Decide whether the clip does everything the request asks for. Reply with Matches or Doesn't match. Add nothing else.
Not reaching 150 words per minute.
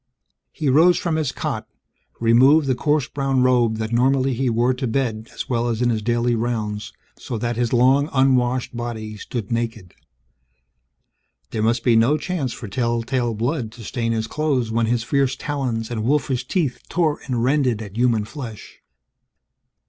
Doesn't match